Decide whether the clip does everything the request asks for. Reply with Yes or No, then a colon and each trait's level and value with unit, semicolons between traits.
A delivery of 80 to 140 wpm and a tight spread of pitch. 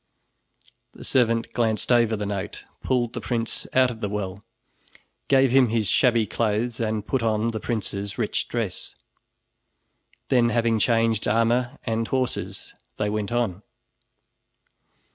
Yes: slow, 135 wpm; narrow, 2.2 semitones